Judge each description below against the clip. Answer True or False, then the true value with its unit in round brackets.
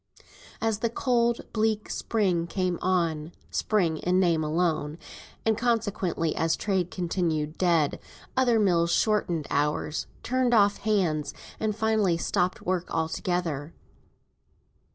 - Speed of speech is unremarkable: False (115 wpm)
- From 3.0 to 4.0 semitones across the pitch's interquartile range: False (4.8 semitones)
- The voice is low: False (180 Hz)